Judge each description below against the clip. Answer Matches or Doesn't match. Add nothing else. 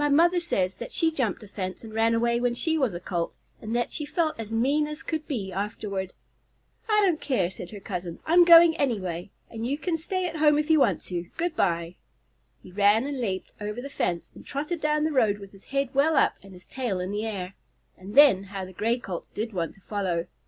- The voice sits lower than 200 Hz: Doesn't match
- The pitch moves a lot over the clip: Matches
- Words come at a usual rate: Doesn't match